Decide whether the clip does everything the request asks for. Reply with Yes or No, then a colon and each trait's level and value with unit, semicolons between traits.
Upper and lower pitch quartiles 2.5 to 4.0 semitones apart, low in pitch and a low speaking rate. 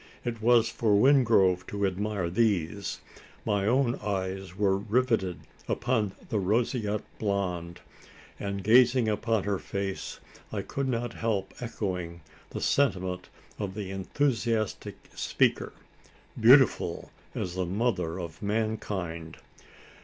Yes: average, 3.6 semitones; low, 105 Hz; slow, 115 wpm